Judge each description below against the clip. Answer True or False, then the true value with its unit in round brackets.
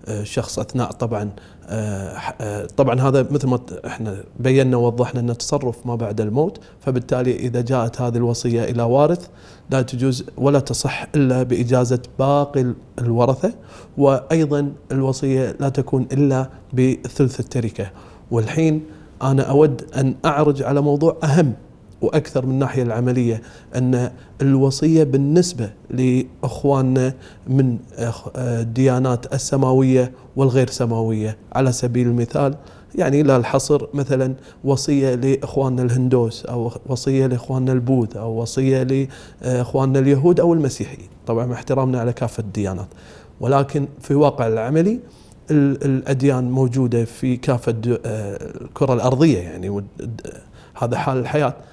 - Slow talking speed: True (115 wpm)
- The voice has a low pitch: True (130 Hz)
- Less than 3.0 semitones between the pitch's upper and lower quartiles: True (2.5 semitones)